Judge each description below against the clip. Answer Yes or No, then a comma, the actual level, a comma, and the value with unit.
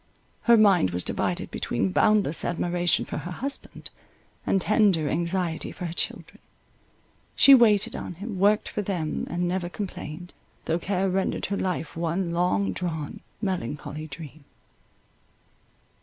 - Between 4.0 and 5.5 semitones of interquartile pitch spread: No, average, 3.5 semitones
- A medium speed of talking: No, slow, 130 wpm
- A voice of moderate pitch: Yes, medium, 175 Hz